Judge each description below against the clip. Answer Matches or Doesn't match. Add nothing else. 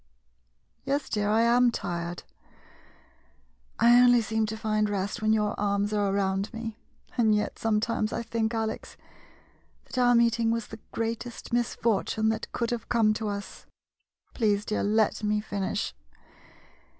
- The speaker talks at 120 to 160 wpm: Matches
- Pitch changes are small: Matches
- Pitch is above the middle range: Matches